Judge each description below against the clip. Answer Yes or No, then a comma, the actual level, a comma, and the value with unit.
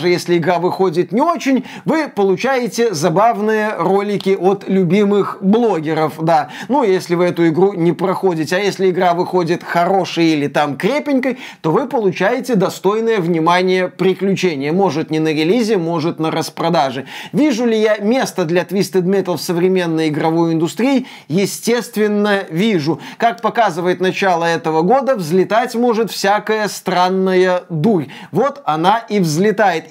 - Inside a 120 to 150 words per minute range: Yes, average, 140 wpm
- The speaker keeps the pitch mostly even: No, average, 3.8 semitones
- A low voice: No, medium, 185 Hz